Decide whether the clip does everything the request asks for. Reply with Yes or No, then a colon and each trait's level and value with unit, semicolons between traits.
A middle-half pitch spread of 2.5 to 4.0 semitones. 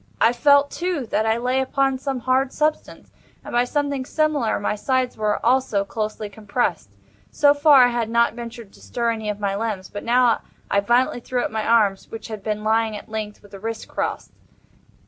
Yes: average, 3.3 semitones